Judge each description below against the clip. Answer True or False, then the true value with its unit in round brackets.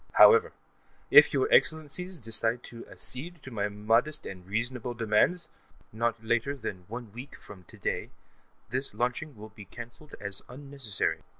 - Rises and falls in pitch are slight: False (4.5 semitones)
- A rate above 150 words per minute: False (145 wpm)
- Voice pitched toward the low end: True (120 Hz)